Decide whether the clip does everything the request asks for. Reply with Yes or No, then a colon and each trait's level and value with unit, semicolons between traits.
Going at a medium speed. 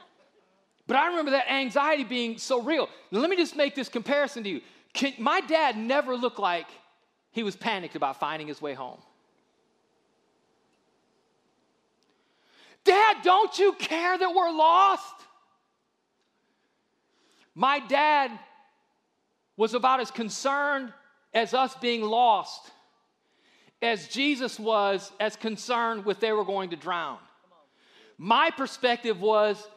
No: slow, 125 wpm